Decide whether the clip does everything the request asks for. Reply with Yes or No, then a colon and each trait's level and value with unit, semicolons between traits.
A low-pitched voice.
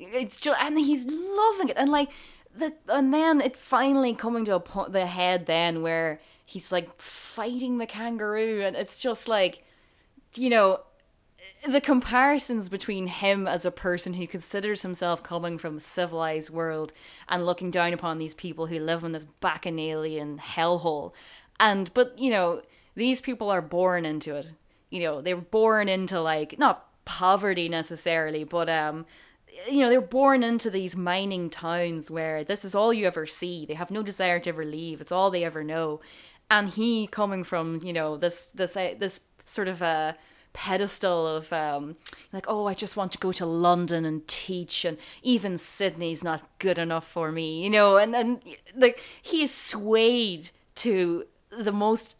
No: medium, 185 Hz